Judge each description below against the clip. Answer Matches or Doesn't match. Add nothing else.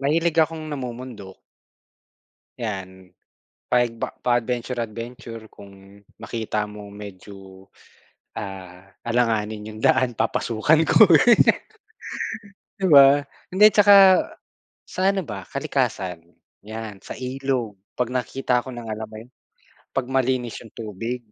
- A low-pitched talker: Matches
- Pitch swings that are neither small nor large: Matches